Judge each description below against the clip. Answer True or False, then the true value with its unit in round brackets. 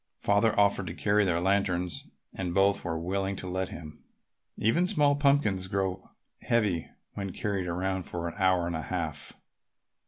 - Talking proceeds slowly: False (160 wpm)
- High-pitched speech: False (95 Hz)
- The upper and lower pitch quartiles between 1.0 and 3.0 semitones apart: True (2.5 semitones)